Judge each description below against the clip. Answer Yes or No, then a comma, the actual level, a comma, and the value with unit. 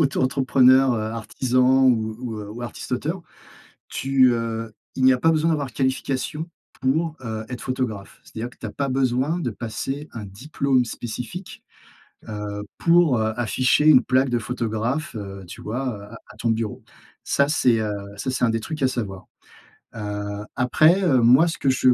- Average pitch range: Yes, average, 3.5 semitones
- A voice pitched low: Yes, low, 125 Hz